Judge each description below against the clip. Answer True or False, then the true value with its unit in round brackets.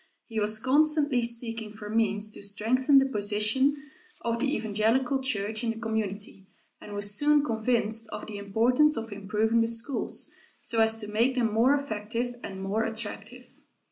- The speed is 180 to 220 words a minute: False (165 wpm)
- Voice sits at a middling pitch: False (225 Hz)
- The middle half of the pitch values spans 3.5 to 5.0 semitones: False (3.1 semitones)